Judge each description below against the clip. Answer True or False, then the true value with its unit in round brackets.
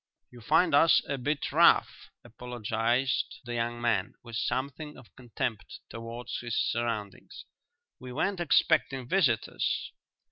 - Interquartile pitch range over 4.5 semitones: False (2.8 semitones)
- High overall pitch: False (120 Hz)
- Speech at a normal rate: False (120 wpm)